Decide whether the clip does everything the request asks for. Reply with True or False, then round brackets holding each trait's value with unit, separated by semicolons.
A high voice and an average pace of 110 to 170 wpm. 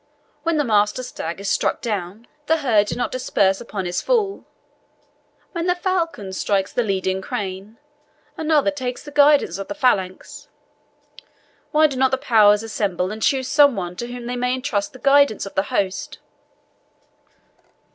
True (240 Hz; 165 wpm)